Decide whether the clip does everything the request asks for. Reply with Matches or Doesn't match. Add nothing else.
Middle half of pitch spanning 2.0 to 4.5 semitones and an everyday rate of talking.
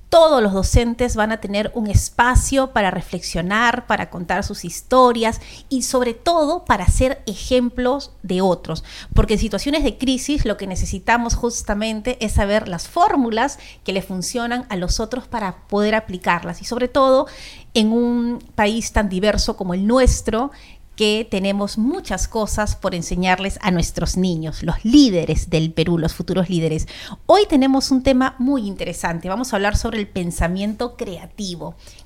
Doesn't match